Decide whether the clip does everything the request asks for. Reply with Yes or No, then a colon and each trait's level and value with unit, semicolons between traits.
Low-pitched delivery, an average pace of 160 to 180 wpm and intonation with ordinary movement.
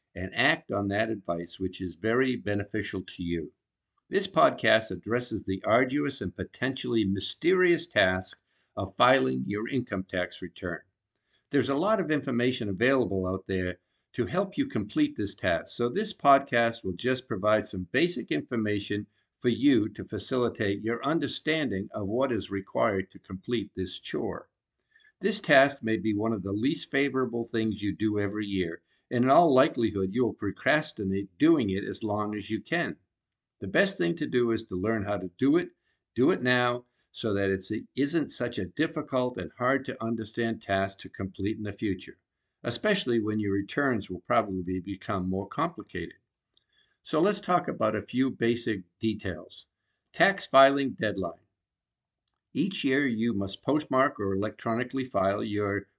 Yes: low, 110 Hz; average, 165 wpm; average, 4.8 semitones